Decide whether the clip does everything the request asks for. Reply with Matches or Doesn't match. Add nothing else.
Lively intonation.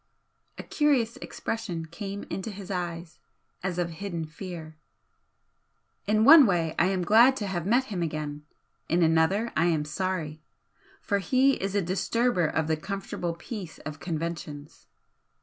Doesn't match